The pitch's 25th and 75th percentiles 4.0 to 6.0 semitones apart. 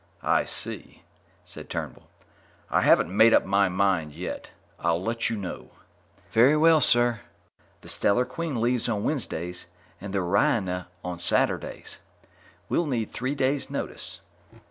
Yes: wide, 5.6 semitones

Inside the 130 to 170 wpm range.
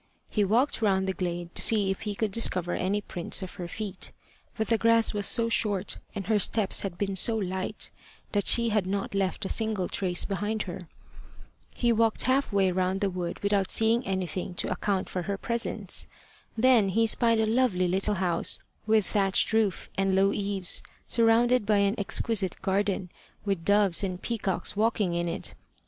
No: average, 185 wpm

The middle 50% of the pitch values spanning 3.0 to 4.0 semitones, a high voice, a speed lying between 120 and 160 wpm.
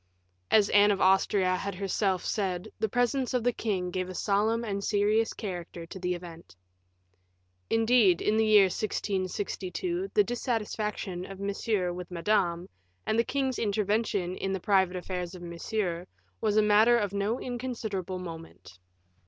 Yes: average, 3.3 semitones; high, 200 Hz; average, 155 wpm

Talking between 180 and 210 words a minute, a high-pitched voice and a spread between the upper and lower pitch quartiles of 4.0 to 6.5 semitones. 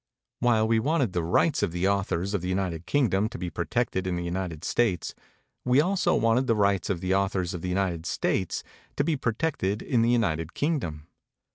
No: fast, 205 wpm; low, 100 Hz; average, 5.0 semitones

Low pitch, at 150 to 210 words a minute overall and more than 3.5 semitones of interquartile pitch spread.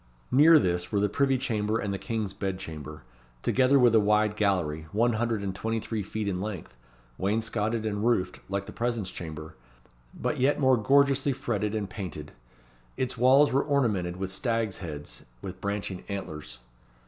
Yes: low, 105 Hz; average, 170 wpm; average, 4.0 semitones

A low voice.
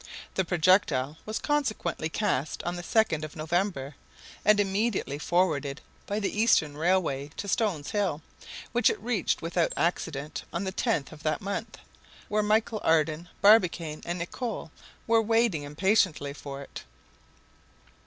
No: medium, 175 Hz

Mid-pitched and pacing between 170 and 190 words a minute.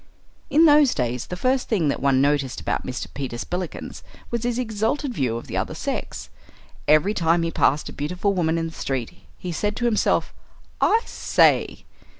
Yes: medium, 170 Hz; average, 180 wpm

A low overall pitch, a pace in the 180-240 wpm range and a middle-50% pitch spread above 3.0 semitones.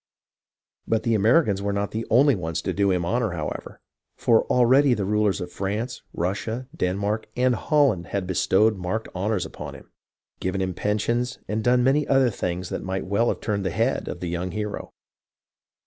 Yes: low, 105 Hz; average, 185 wpm; average, 4.1 semitones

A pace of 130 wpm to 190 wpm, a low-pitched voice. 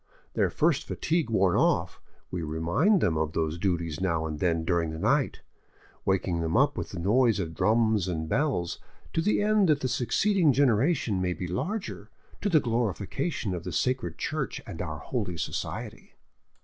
Yes: average, 175 wpm; low, 100 Hz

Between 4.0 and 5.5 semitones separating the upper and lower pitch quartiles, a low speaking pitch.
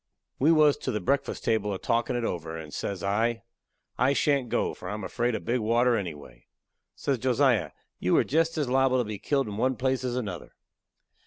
Yes: average, 4.4 semitones; low, 120 Hz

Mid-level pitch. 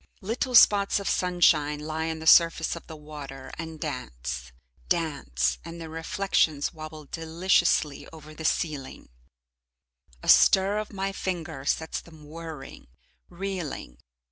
Yes: medium, 160 Hz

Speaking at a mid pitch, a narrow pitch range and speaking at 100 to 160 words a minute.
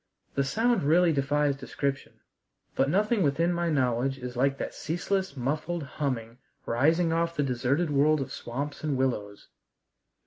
No: medium, 145 Hz; average, 3.9 semitones; average, 145 wpm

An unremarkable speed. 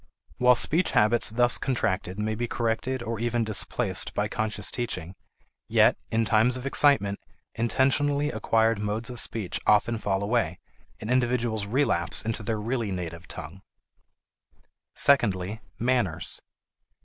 No: slow, 130 wpm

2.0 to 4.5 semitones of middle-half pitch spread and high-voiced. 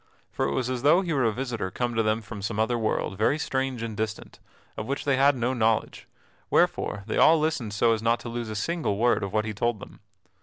No: average, 3.3 semitones; low, 115 Hz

